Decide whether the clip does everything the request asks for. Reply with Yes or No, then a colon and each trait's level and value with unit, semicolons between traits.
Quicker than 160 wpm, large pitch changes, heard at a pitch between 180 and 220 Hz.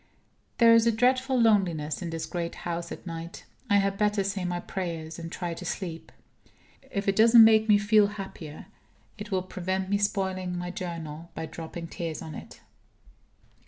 No: average, 175 wpm; average, 3.6 semitones; medium, 185 Hz